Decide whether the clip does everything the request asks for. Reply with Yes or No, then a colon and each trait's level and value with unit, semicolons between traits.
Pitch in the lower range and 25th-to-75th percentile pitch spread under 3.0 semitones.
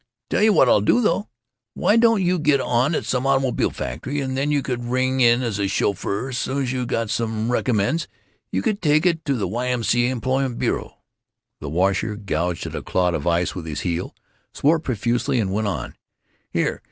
No: low, 125 Hz; average, 4.9 semitones